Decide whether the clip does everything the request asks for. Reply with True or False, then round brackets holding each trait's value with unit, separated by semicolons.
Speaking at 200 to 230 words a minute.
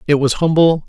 True (205 wpm)